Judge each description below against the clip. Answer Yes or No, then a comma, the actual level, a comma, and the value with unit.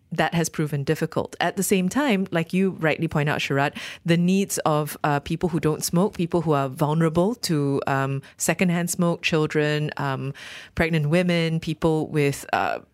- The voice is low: No, medium, 160 Hz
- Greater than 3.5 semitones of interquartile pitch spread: No, average, 2.7 semitones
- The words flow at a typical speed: Yes, average, 170 wpm